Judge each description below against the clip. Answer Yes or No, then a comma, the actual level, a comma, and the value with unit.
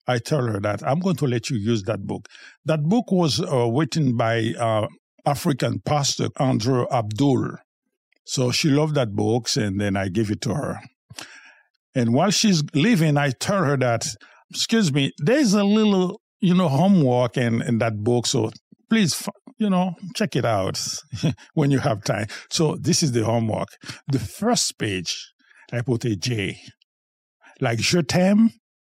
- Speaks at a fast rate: No, average, 170 wpm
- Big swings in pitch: Yes, wide, 6.8 semitones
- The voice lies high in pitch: No, low, 135 Hz